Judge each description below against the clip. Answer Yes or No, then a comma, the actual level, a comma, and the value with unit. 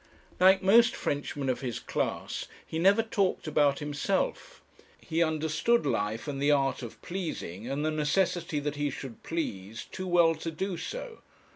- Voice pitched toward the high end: No, medium, 155 Hz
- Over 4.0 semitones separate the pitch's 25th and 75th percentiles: Yes, average, 4.8 semitones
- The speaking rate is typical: Yes, average, 160 wpm